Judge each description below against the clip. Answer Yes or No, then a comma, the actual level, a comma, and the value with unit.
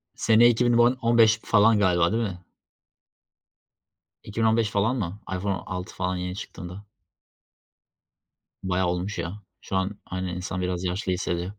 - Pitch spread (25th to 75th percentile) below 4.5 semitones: Yes, average, 3.5 semitones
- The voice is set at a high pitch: No, very low, 95 Hz